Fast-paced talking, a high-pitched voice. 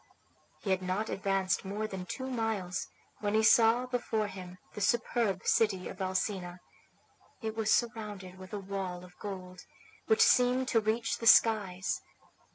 No: average, 155 wpm; high, 205 Hz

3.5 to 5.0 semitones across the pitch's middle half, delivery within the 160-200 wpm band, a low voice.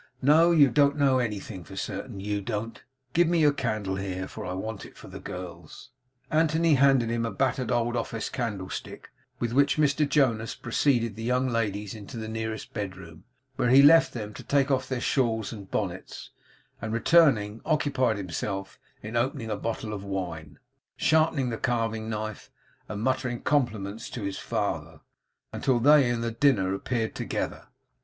Yes: average, 4.6 semitones; average, 165 wpm; low, 115 Hz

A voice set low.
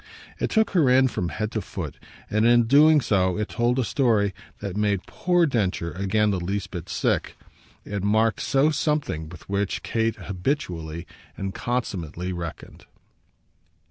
Yes: low, 105 Hz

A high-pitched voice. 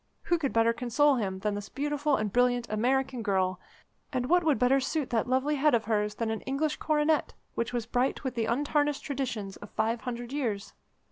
Yes: high, 245 Hz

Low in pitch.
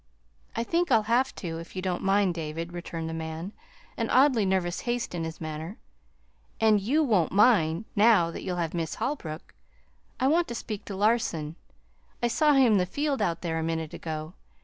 No: medium, 185 Hz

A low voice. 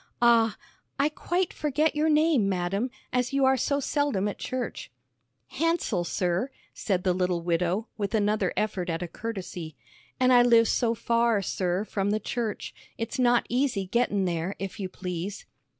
No: high, 215 Hz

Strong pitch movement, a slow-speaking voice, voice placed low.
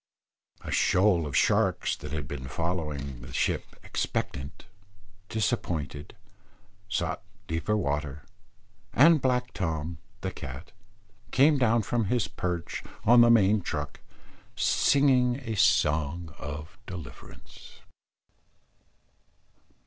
Yes: wide, 7.5 semitones; slow, 105 wpm; very low, 90 Hz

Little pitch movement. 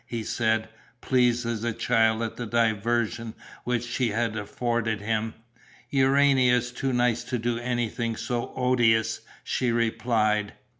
Yes: narrow, 1.6 semitones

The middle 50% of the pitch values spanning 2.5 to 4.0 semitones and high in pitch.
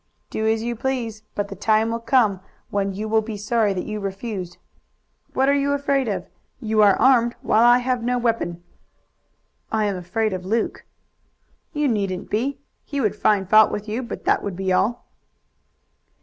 Yes: average, 3.1 semitones; high, 220 Hz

